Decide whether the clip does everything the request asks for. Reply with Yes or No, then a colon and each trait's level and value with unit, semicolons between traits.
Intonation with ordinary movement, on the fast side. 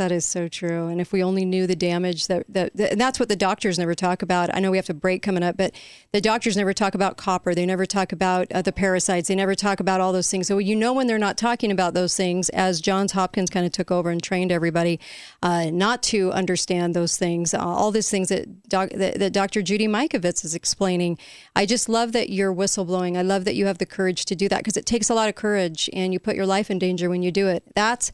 No: narrow, 1.8 semitones; fast, 265 wpm